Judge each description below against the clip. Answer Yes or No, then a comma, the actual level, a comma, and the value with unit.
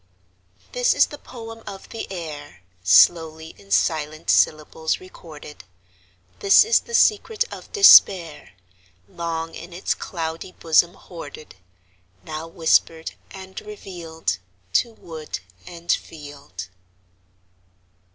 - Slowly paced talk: Yes, slow, 105 wpm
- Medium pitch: Yes, medium, 165 Hz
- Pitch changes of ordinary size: Yes, average, 3.6 semitones